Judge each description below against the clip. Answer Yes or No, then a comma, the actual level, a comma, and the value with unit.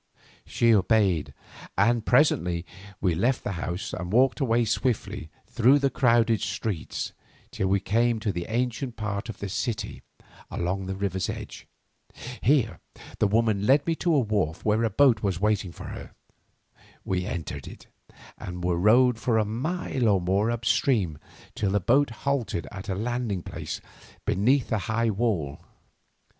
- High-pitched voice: No, low, 110 Hz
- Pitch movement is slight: No, average, 4.0 semitones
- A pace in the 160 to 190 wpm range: Yes, average, 165 wpm